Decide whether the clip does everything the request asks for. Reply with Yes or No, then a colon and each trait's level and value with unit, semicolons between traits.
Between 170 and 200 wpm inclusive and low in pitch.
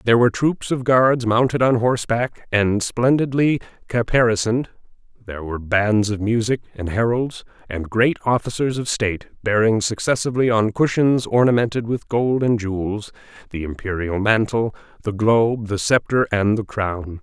No: average, 145 wpm; low, 115 Hz